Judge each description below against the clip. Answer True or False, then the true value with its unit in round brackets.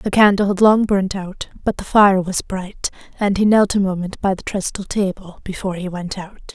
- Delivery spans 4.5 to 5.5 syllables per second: True (5.1 syllables/s)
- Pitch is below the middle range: False (195 Hz)